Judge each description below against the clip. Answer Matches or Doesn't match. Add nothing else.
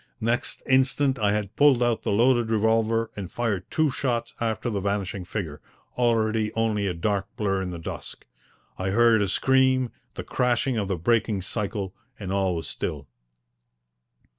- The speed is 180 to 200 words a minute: Doesn't match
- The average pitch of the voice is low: Matches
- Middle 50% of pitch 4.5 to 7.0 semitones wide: Doesn't match